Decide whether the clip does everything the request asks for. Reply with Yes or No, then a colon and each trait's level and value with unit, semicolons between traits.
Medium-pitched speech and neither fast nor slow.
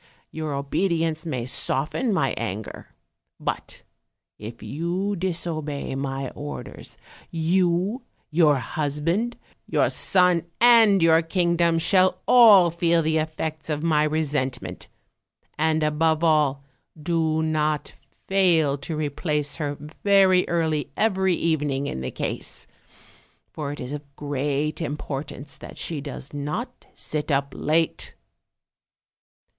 No: medium, 155 Hz; slow, 120 wpm